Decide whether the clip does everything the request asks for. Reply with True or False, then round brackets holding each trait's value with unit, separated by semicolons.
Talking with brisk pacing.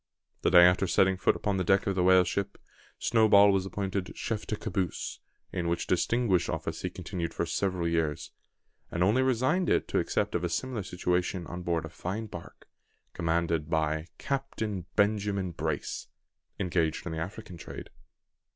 False (170 wpm)